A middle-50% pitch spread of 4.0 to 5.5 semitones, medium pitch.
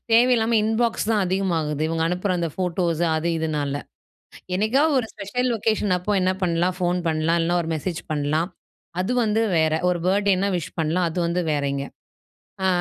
Yes: average, 4.4 semitones; medium, 180 Hz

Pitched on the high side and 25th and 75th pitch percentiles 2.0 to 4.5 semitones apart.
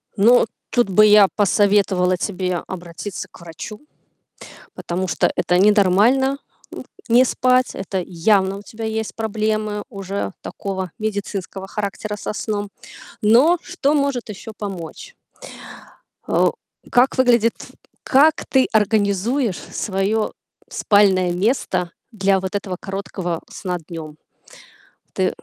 Yes: high, 205 Hz; average, 2.9 semitones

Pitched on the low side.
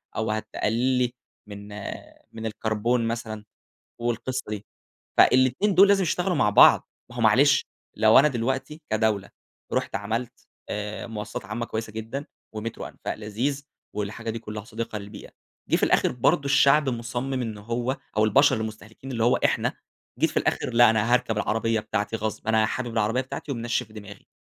Yes: low, 115 Hz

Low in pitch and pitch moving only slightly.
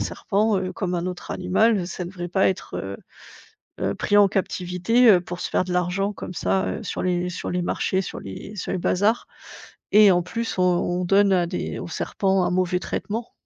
No: medium, 185 Hz; narrow, 2.1 semitones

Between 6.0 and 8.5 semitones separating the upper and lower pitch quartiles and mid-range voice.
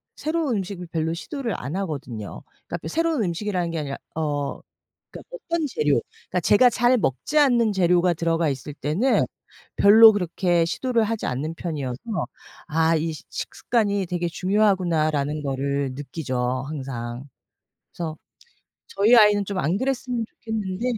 Yes: wide, 6.5 semitones; medium, 175 Hz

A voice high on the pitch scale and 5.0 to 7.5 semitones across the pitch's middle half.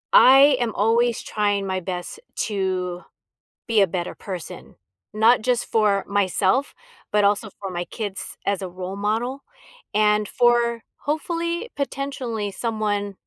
No: high, 210 Hz; average, 3.6 semitones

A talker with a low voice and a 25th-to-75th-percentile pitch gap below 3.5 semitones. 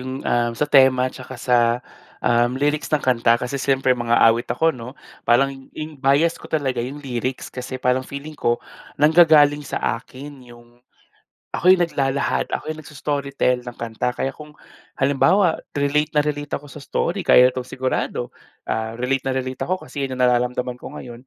Yes: low, 130 Hz; average, 2.8 semitones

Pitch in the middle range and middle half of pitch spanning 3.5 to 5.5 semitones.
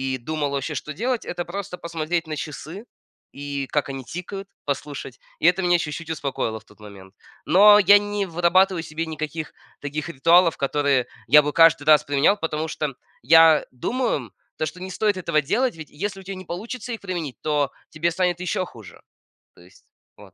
Yes: medium, 160 Hz; average, 4.2 semitones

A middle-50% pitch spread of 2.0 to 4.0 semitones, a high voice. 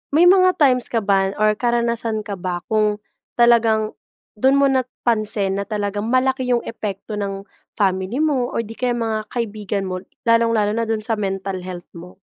Yes: average, 3.1 semitones; high, 215 Hz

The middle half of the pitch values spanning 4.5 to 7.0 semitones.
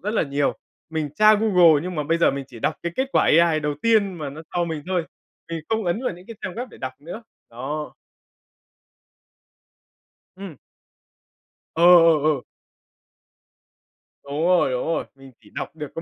No: average, 4.0 semitones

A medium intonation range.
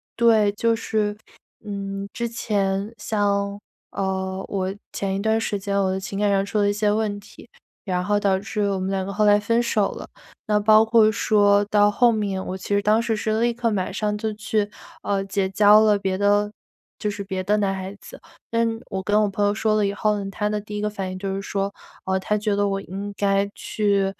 No: narrow, 1.4 semitones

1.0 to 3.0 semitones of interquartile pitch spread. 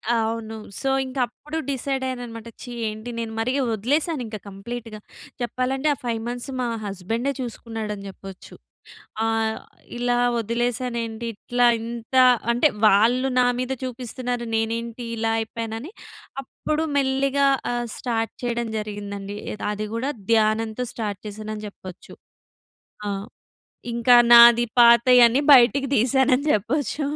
Yes: narrow, 2.4 semitones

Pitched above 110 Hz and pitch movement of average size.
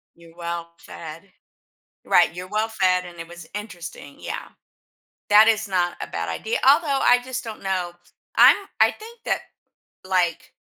Yes: medium, 185 Hz; average, 4.3 semitones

